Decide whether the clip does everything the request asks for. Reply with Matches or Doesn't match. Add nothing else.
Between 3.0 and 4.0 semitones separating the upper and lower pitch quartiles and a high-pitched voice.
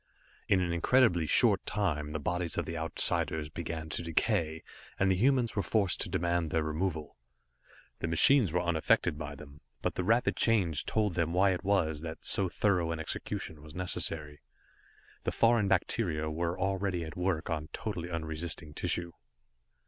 Doesn't match